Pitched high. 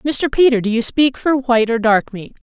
Yes: high, 245 Hz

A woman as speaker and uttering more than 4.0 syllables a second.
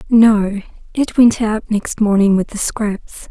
No: female; 3.8 syllables/s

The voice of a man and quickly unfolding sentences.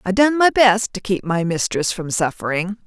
No: female; fast, 210 wpm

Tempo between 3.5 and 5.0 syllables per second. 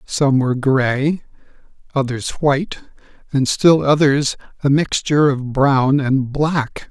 Yes: 3.8 syllables/s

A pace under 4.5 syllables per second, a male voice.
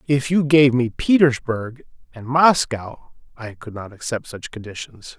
Yes: 4.2 syllables/s; male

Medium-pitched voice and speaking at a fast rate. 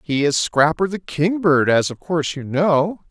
No: medium, 160 Hz; average, 195 wpm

